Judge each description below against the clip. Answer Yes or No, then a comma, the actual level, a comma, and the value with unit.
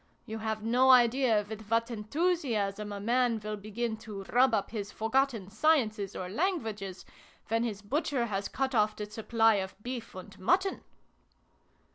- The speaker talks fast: No, average, 155 wpm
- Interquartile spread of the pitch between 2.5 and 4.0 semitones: Yes, average, 3.2 semitones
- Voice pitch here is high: Yes, high, 220 Hz